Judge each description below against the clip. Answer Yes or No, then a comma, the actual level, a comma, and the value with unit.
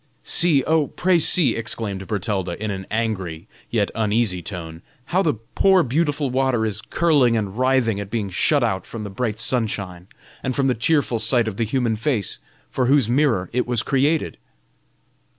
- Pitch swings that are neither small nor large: Yes, average, 4.7 semitones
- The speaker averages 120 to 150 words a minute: No, average, 170 wpm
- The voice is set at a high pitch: No, low, 115 Hz